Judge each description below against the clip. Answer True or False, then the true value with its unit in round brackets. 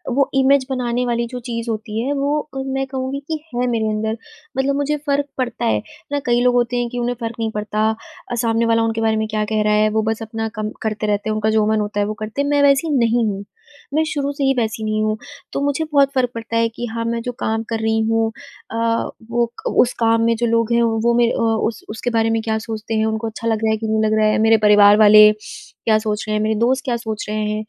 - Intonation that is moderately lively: False (2.2 semitones)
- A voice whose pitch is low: False (225 Hz)